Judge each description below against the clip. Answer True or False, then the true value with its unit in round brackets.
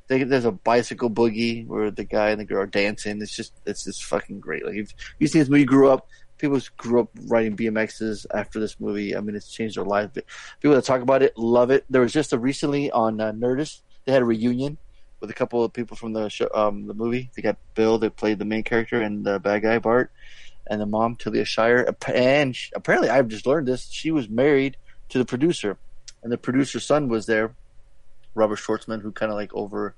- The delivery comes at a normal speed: False (230 wpm)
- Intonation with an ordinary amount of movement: True (3.1 semitones)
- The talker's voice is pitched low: True (115 Hz)